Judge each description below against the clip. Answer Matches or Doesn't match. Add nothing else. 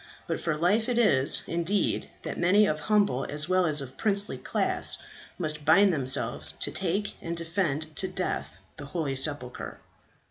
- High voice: Doesn't match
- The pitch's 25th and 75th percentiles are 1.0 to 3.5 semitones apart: Doesn't match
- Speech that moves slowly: Doesn't match